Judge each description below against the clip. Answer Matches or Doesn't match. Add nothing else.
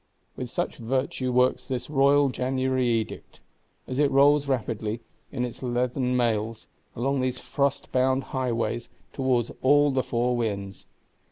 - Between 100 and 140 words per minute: Matches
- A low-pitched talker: Matches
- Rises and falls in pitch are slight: Matches